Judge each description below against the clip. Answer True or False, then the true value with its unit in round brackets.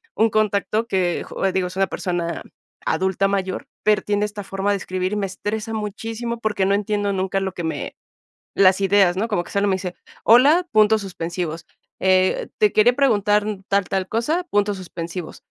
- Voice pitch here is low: False (200 Hz)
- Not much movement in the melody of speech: True (2.2 semitones)